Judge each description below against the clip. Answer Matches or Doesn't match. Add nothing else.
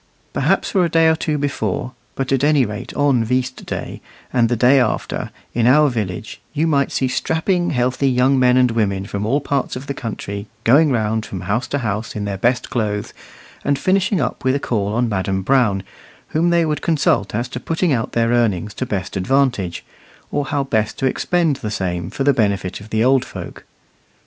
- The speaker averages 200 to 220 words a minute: Matches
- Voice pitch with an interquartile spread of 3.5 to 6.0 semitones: Matches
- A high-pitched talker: Doesn't match